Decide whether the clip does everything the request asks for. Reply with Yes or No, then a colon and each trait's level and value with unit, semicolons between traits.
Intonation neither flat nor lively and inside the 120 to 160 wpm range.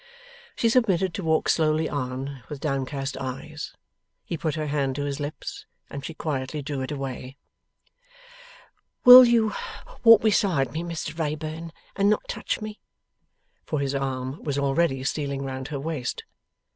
Yes: average, 3.5 semitones; average, 150 wpm